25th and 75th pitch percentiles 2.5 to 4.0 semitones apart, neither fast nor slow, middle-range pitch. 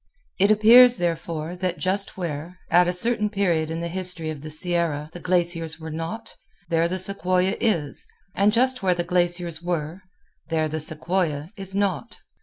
Yes: average, 2.9 semitones; average, 170 wpm; medium, 175 Hz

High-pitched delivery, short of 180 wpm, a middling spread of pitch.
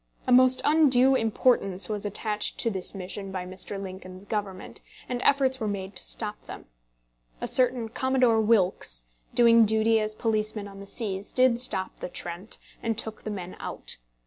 Yes: high, 215 Hz; average, 170 wpm; average, 3.5 semitones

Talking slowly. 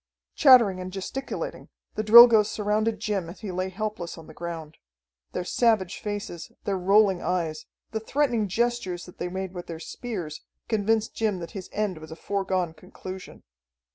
No: average, 165 wpm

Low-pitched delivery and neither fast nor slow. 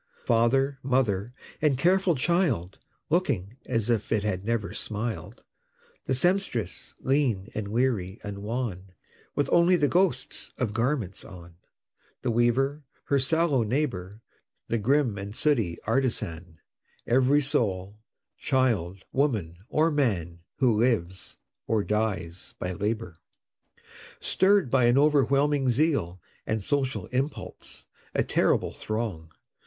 No: low, 120 Hz; slow, 120 wpm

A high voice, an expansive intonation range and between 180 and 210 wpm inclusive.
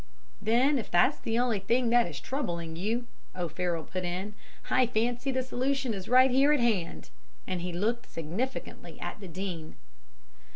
No: high, 225 Hz; wide, 6.0 semitones; average, 165 wpm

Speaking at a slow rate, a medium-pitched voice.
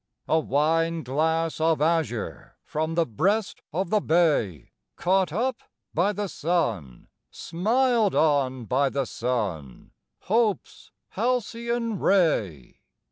Yes: slow, 110 wpm; medium, 165 Hz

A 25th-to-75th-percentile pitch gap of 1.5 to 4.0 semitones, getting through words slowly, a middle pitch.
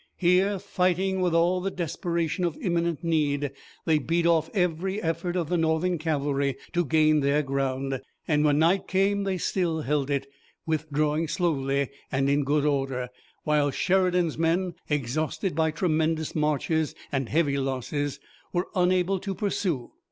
No: average, 3.6 semitones; average, 150 wpm; medium, 160 Hz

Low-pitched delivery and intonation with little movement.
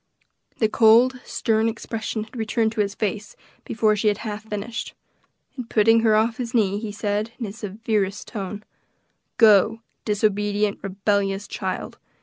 No: high, 215 Hz; narrow, 1.6 semitones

